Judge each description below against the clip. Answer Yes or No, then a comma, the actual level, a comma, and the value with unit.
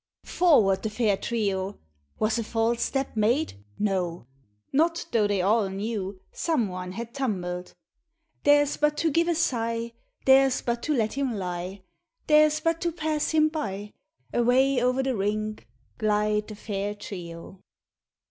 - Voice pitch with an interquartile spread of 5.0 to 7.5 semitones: Yes, wide, 5.6 semitones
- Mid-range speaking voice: No, high, 225 Hz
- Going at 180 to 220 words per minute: No, average, 150 wpm